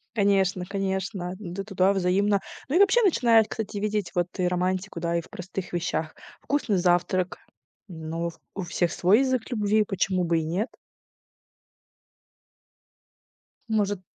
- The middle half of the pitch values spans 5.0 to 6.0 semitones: No, average, 2.9 semitones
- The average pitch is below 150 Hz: No, high, 190 Hz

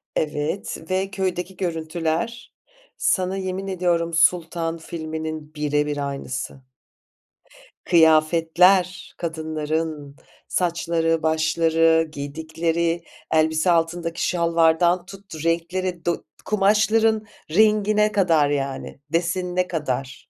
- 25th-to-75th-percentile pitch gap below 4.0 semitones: Yes, narrow, 2.5 semitones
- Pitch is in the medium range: Yes, medium, 165 Hz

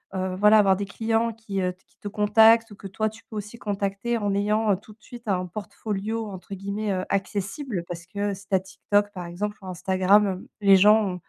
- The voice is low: No, high, 205 Hz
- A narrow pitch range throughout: Yes, narrow, 2.2 semitones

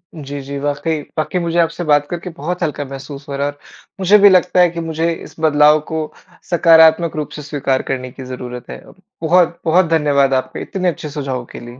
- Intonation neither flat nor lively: Yes, average, 3.2 semitones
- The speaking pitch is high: No, medium, 155 Hz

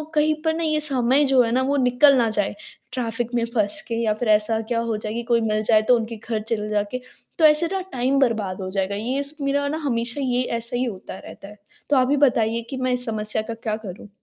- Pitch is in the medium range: No, high, 235 Hz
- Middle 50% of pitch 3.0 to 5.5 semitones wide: Yes, average, 3.6 semitones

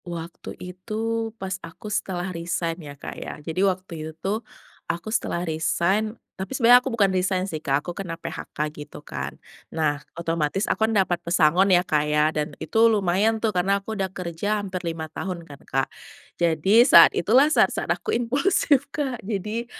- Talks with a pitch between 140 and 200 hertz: Yes, medium, 185 Hz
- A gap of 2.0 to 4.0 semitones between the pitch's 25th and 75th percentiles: No, average, 4.5 semitones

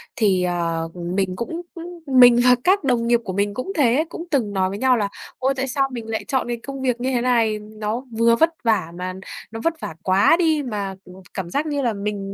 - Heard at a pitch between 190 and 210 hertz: No, high, 235 Hz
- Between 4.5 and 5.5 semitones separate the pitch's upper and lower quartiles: Yes, average, 5.0 semitones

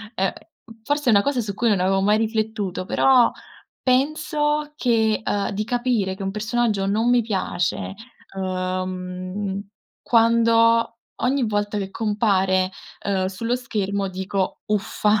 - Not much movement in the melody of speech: No, average, 3.4 semitones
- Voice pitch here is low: No, high, 210 Hz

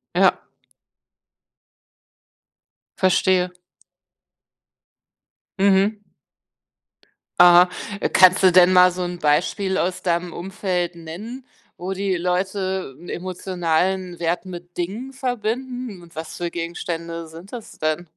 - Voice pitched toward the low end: No, medium, 180 Hz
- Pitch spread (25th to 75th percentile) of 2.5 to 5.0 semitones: No, narrow, 1.9 semitones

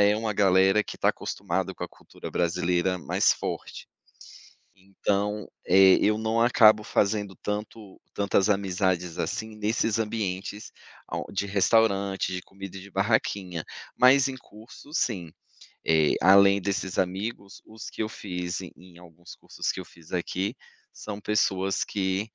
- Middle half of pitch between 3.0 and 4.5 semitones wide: No, narrow, 2.4 semitones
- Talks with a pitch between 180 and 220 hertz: No, low, 100 Hz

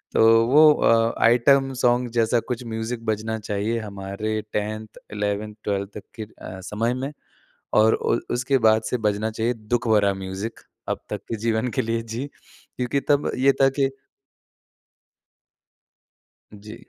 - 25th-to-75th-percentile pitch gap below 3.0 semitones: Yes, narrow, 2.5 semitones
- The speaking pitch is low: Yes, low, 110 Hz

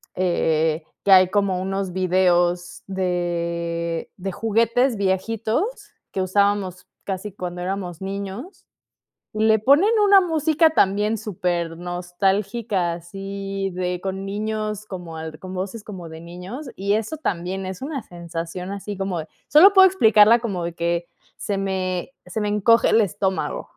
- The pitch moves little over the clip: No, average, 3.2 semitones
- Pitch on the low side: No, high, 195 Hz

